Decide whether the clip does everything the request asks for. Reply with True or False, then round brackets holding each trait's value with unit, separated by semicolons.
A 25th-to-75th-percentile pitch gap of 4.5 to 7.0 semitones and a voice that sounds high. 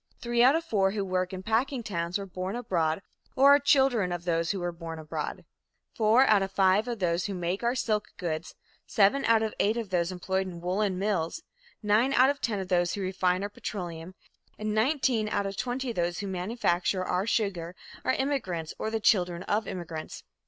False (4.1 semitones; 195 Hz)